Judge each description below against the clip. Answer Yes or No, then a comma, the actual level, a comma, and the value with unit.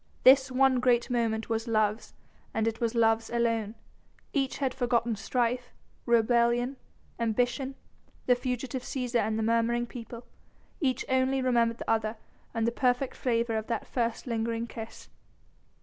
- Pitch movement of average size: No, narrow, 1.8 semitones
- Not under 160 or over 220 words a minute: No, average, 145 wpm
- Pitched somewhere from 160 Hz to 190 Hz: No, high, 235 Hz